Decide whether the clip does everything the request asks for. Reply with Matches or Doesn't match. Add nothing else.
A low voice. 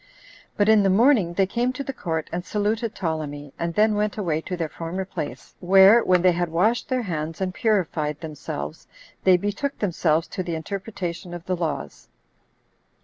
Doesn't match